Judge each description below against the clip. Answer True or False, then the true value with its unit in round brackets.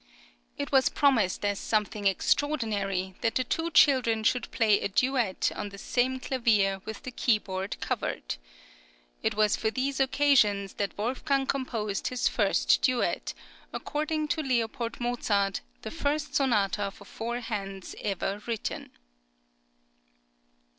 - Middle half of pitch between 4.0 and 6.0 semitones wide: True (4.5 semitones)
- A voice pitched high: True (230 Hz)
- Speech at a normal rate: False (130 wpm)